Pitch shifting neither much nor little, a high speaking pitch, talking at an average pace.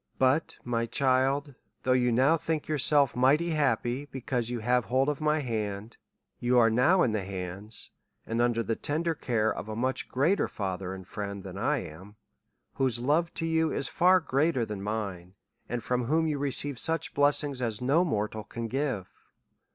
No: average, 4.9 semitones; low, 125 Hz; average, 180 wpm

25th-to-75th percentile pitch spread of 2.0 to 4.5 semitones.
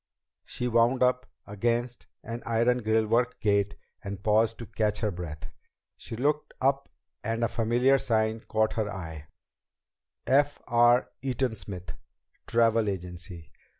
Yes: average, 2.9 semitones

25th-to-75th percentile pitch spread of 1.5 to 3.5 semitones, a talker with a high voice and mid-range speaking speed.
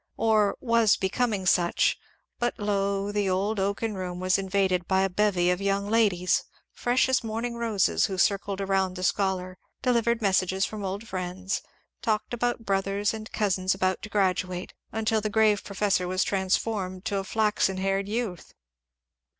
Yes: narrow, 2.5 semitones; high, 200 Hz; average, 160 wpm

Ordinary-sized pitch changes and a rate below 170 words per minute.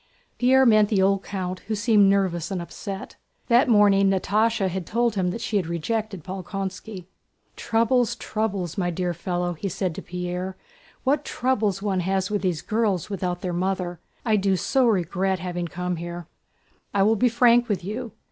No: average, 3.3 semitones; average, 175 wpm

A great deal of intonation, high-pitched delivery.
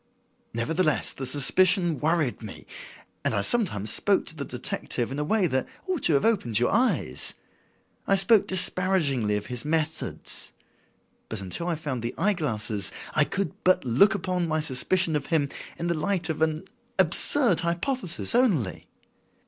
No: wide, 6.3 semitones; medium, 160 Hz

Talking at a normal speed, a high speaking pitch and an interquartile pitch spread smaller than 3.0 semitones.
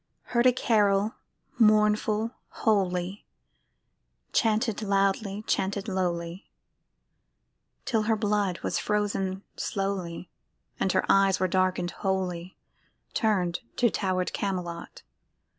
No: slow, 100 wpm; high, 195 Hz; narrow, 2.4 semitones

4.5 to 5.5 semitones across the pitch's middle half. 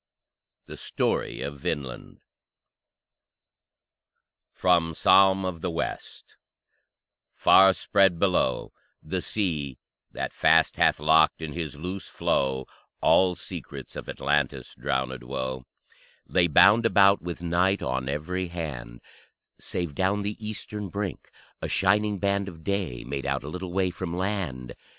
Yes: average, 5.2 semitones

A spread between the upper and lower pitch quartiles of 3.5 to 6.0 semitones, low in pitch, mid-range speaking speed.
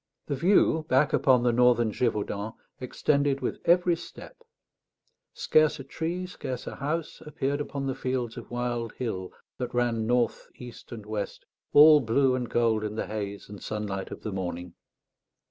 Yes: average, 4.5 semitones; low, 125 Hz; average, 165 wpm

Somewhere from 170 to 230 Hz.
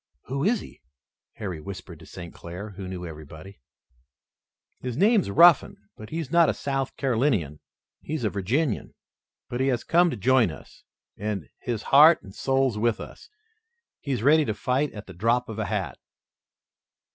No: low, 120 Hz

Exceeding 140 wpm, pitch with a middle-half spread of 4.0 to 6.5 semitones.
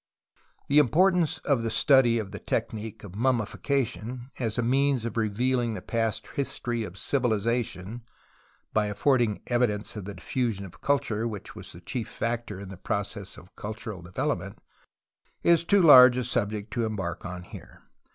No: average, 160 wpm; average, 3.5 semitones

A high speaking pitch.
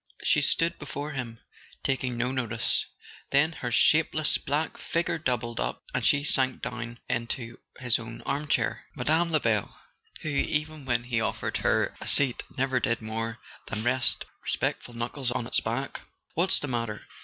No: low, 125 Hz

